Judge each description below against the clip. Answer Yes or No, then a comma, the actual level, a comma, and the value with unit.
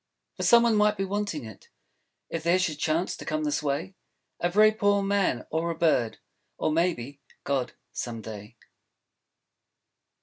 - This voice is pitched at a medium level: Yes, medium, 165 Hz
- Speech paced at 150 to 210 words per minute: Yes, average, 160 wpm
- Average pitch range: No, wide, 6.1 semitones